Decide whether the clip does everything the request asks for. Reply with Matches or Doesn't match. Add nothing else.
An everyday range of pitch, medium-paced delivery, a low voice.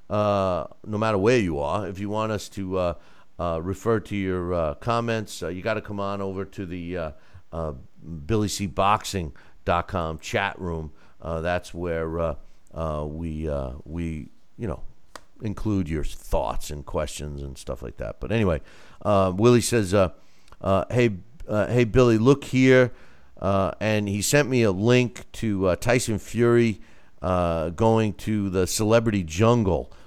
Matches